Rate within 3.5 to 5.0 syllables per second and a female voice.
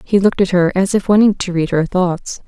No: 5.5 syllables/s; female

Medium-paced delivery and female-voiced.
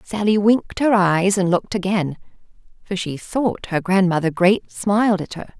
Yes: average, 170 wpm; female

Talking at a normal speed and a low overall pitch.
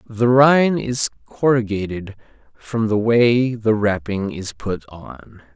No: slow, 130 wpm; low, 110 Hz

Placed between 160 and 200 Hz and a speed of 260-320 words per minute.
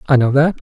No: medium, 140 Hz; fast, 270 wpm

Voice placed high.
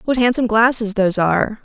Yes: high, 220 Hz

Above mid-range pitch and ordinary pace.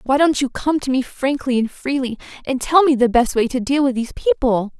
No: very high, 260 Hz; fast, 250 wpm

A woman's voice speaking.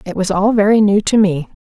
Yes: female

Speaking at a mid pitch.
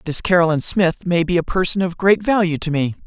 Yes: medium, 175 Hz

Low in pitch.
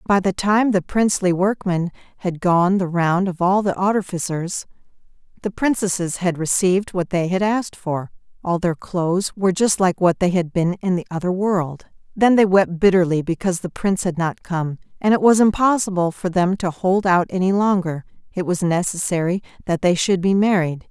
No: medium, 185 Hz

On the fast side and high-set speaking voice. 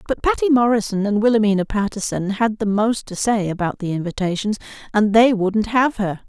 No: average, 180 wpm; high, 210 Hz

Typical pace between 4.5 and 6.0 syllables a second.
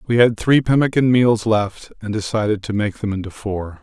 Yes: 5.0 syllables/s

